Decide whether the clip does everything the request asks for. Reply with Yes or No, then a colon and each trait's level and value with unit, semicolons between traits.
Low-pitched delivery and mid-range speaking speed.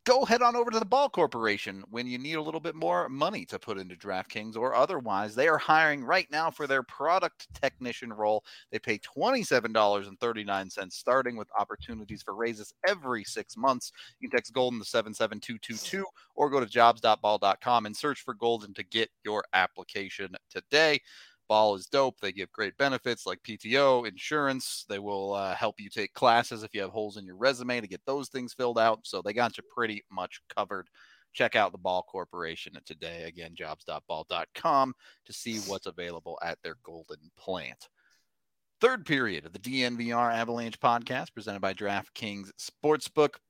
Yes: low, 115 Hz; average, 185 wpm